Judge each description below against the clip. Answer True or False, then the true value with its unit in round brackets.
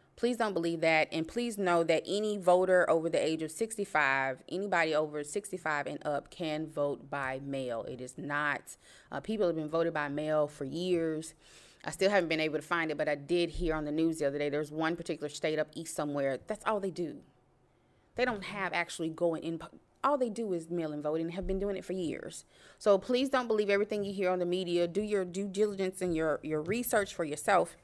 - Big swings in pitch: False (4.2 semitones)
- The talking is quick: True (225 wpm)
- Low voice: False (165 Hz)